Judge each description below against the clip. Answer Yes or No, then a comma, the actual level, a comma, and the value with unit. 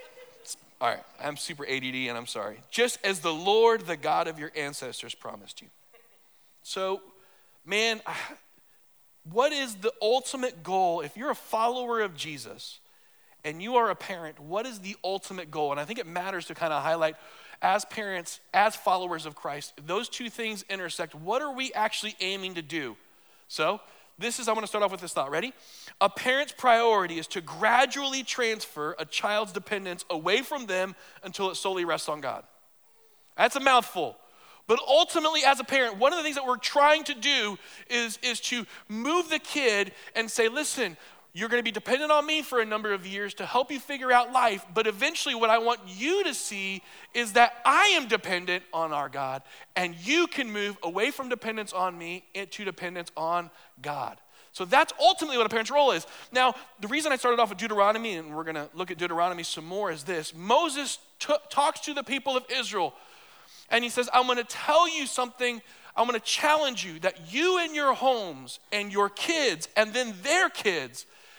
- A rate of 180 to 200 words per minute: Yes, average, 195 wpm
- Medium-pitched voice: No, high, 225 Hz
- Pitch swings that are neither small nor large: No, wide, 6.2 semitones